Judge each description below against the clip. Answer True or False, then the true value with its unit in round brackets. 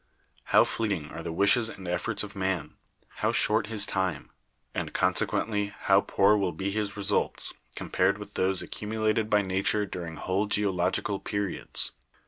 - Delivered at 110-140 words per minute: False (150 wpm)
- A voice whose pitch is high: False (100 Hz)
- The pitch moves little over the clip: True (2.0 semitones)